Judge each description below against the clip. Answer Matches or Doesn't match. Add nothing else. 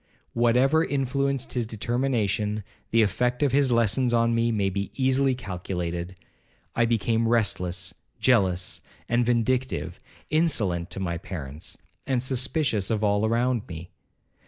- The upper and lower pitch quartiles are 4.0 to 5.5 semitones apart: Matches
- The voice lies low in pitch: Matches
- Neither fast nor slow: Doesn't match